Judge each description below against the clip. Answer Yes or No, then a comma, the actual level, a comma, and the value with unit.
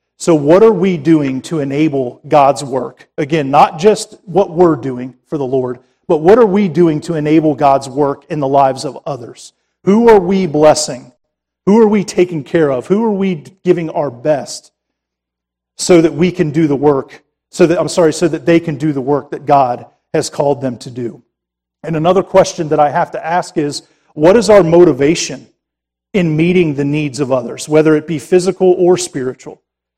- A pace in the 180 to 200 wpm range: Yes, average, 195 wpm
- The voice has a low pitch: No, medium, 155 Hz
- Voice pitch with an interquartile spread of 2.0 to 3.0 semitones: No, average, 4.3 semitones